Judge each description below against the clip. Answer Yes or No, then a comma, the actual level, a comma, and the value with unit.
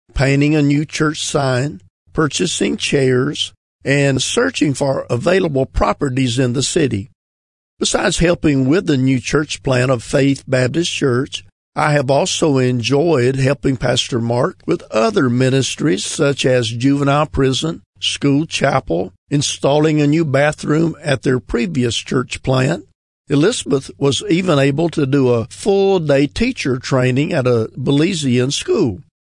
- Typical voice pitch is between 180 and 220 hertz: No, medium, 140 Hz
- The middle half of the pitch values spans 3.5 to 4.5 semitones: No, average, 2.9 semitones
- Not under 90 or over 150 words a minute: Yes, slow, 135 wpm